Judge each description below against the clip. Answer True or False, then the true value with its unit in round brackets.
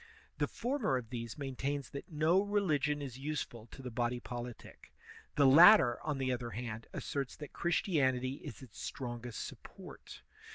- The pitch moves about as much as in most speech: True (3.7 semitones)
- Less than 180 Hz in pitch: True (135 Hz)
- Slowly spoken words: False (155 wpm)